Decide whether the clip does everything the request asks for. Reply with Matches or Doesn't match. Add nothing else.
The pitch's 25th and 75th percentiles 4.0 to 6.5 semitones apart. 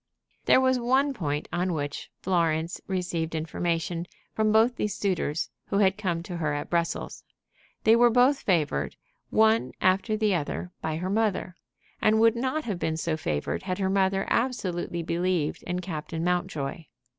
Matches